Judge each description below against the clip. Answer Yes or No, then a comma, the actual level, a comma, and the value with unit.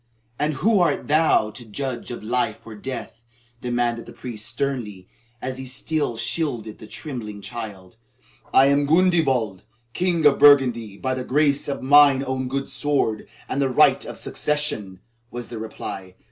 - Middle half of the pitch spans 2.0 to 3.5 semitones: No, average, 4.3 semitones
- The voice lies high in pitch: No, low, 130 Hz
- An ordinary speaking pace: Yes, average, 160 wpm